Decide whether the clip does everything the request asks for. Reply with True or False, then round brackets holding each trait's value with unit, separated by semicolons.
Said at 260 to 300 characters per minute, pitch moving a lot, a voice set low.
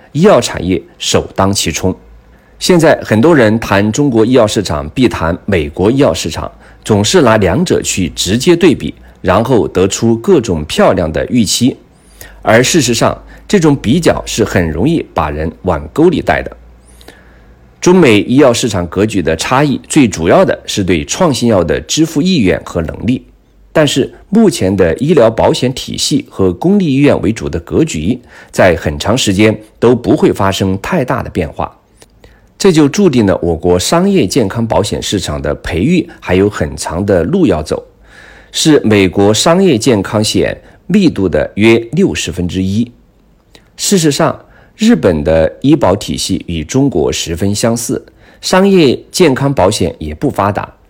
False (240 characters per minute; 6.3 semitones; 100 Hz)